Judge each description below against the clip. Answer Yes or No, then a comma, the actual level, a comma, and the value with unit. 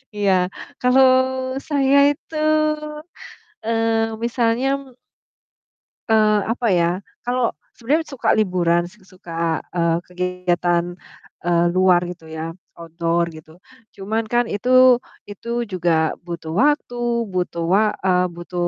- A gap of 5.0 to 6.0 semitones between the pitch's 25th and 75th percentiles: Yes, average, 5.3 semitones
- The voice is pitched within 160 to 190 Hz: Yes, medium, 185 Hz